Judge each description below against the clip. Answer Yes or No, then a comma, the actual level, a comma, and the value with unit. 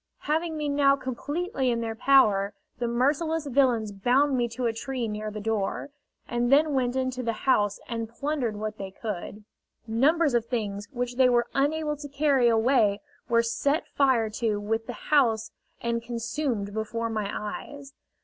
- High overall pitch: Yes, high, 240 Hz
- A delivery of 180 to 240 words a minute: No, average, 170 wpm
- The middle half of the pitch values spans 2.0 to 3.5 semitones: No, average, 3.9 semitones